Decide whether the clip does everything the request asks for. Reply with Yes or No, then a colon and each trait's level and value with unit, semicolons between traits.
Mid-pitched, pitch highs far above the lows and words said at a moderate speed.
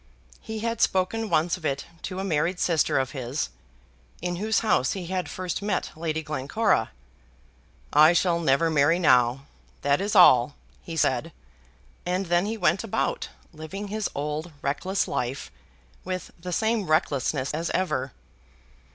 No: medium, 170 Hz; average, 4.7 semitones; average, 150 wpm